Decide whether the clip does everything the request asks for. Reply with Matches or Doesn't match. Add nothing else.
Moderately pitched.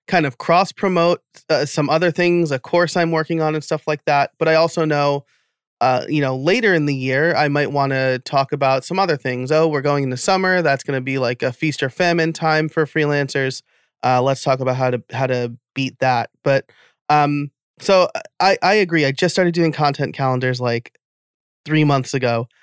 Matches